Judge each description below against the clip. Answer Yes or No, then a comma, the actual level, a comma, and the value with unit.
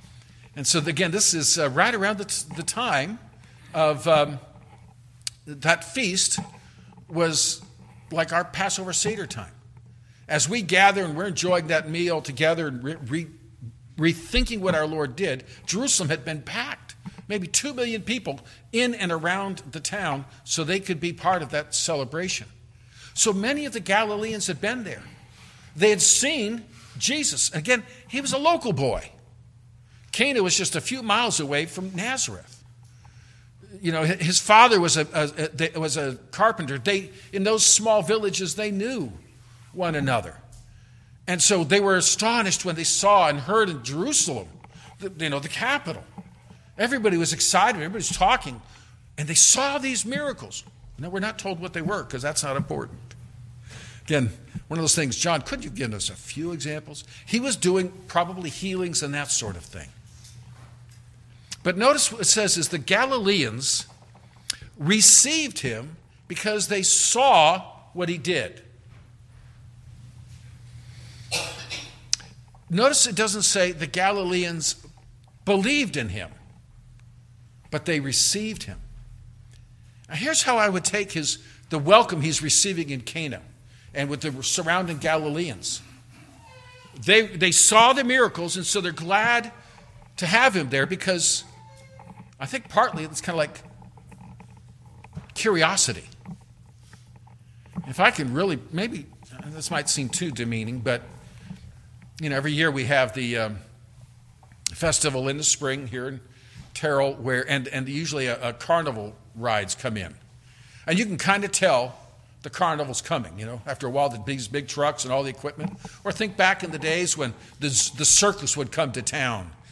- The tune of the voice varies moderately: No, wide, 7.5 semitones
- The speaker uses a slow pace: No, average, 155 wpm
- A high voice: No, medium, 155 Hz